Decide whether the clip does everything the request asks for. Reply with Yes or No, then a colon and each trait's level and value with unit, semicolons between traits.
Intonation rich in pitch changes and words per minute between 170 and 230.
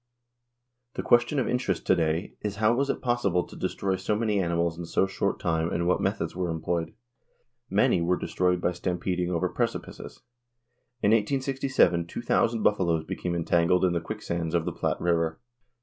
No: average, 3.8 semitones; average, 180 wpm